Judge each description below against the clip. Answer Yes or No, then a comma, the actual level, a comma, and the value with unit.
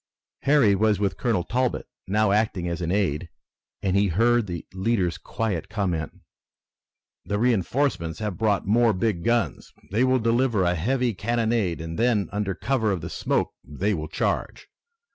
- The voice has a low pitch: Yes, low, 105 Hz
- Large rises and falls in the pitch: No, average, 4.5 semitones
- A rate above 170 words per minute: No, average, 160 wpm